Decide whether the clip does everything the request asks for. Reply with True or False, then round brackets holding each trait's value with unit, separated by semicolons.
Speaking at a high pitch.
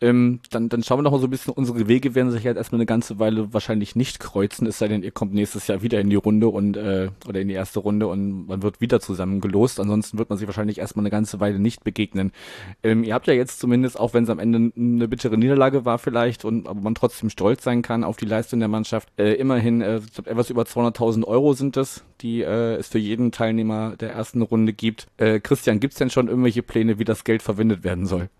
False (115 Hz)